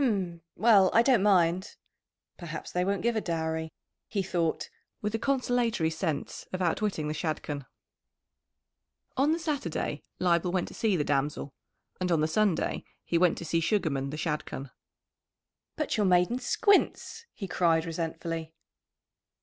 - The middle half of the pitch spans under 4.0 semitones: No, average, 4.7 semitones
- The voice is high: No, medium, 175 Hz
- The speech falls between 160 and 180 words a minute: No, average, 150 wpm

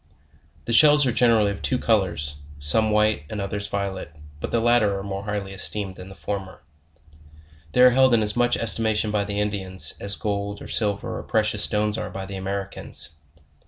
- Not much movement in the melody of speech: Yes, narrow, 2.0 semitones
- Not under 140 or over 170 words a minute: No, average, 190 wpm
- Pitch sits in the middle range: No, low, 105 Hz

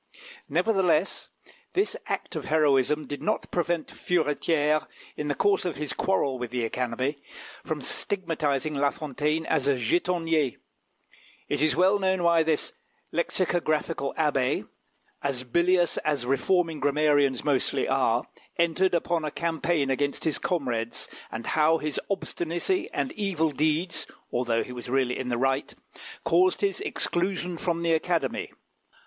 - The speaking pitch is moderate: Yes, medium, 155 Hz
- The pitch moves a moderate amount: Yes, average, 3.8 semitones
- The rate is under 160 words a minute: Yes, average, 140 wpm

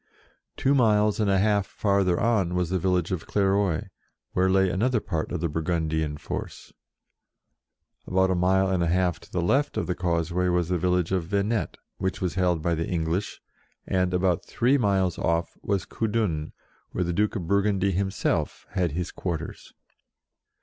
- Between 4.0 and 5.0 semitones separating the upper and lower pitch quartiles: No, narrow, 2.5 semitones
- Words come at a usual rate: Yes, average, 170 wpm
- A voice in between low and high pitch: No, very low, 90 Hz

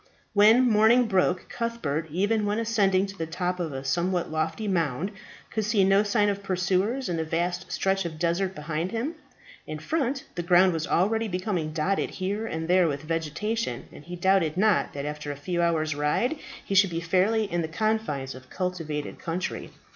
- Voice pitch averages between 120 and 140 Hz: No, medium, 185 Hz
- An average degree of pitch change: Yes, average, 4.3 semitones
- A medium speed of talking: Yes, average, 185 wpm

